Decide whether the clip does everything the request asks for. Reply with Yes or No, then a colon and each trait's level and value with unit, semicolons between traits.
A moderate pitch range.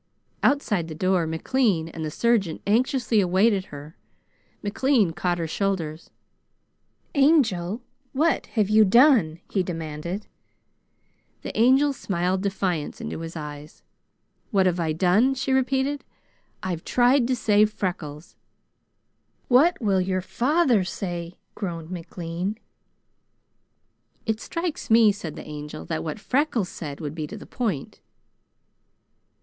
No: wide, 6.2 semitones